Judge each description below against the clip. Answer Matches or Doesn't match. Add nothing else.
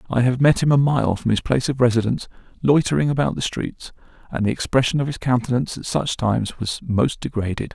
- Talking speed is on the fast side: Matches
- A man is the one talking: Matches